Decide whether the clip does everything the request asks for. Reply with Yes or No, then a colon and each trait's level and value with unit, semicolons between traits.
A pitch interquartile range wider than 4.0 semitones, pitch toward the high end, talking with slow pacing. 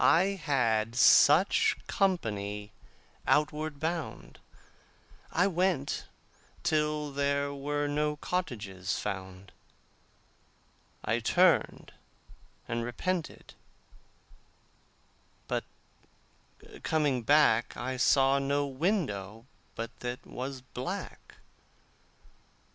No: average, 4.9 semitones; medium, 140 Hz; slow, 75 wpm